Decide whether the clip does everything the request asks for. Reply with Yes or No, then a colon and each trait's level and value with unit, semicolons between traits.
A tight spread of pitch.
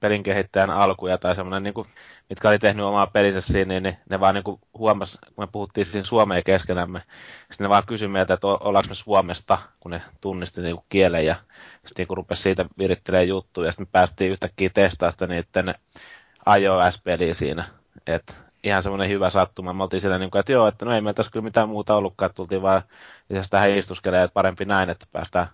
Yes: narrow, 1.5 semitones